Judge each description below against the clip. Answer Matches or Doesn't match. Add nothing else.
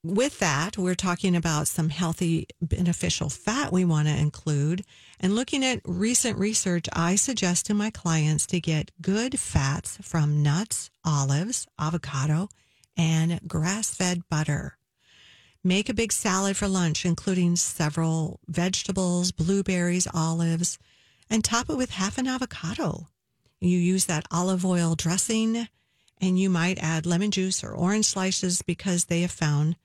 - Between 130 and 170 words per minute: Matches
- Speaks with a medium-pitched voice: Matches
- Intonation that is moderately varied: Matches